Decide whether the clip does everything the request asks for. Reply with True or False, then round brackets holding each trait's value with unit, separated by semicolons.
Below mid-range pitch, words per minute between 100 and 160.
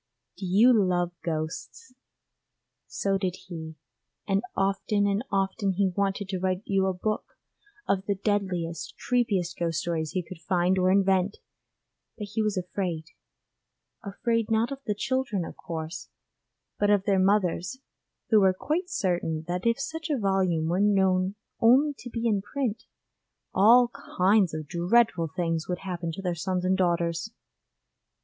False (190 Hz; 155 wpm)